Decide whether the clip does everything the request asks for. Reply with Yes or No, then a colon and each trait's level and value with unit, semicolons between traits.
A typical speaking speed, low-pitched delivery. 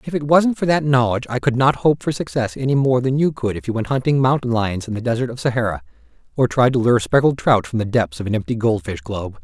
No: fast, 265 wpm; low, 120 Hz